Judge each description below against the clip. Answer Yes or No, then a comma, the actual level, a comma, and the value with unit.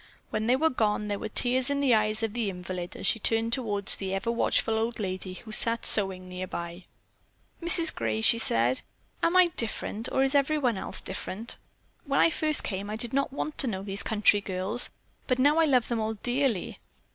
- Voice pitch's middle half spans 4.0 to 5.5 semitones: Yes, average, 5.0 semitones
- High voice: Yes, high, 225 Hz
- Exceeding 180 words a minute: Yes, fast, 205 wpm